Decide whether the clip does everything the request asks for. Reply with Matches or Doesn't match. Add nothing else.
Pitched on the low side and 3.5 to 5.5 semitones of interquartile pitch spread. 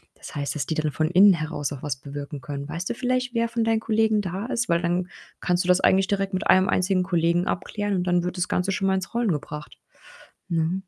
Doesn't match